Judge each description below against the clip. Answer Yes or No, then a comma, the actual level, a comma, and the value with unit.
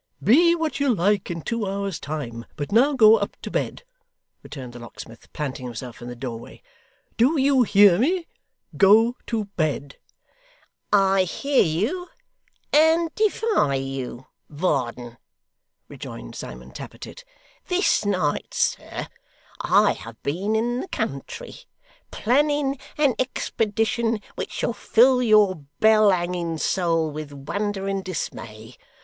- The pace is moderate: No, slow, 130 wpm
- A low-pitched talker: No, high, 200 Hz